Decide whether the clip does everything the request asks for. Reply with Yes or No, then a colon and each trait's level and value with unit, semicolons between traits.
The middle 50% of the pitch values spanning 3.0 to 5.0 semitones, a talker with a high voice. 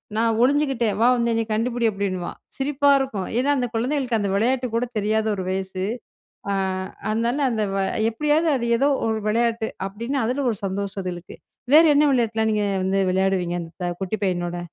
Yes: average, 4.3 semitones; high, 225 Hz